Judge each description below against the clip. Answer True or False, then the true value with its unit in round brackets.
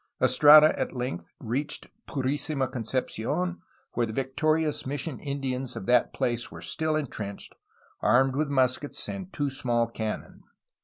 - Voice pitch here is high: False (130 Hz)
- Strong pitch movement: False (3.6 semitones)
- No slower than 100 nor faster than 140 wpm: True (135 wpm)